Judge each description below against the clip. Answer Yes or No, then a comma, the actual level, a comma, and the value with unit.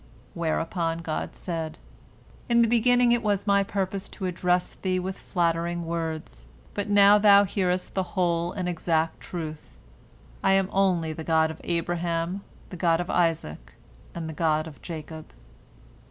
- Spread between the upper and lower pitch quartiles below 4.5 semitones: Yes, average, 2.9 semitones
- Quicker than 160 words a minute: No, average, 155 wpm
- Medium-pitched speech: Yes, medium, 175 Hz